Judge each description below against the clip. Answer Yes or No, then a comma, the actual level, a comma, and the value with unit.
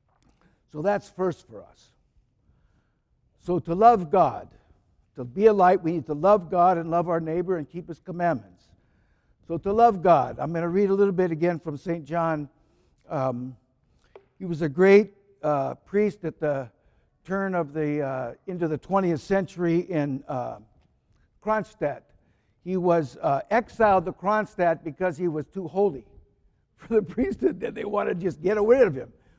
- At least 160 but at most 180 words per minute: Yes, average, 170 wpm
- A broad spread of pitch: No, average, 4.5 semitones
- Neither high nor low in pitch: Yes, medium, 170 Hz